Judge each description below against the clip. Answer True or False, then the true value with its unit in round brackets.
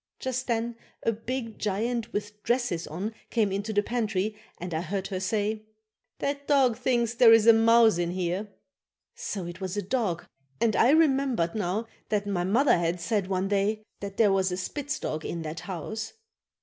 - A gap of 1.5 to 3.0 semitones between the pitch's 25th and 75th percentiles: False (3.8 semitones)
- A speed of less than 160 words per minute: False (185 wpm)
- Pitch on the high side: True (210 Hz)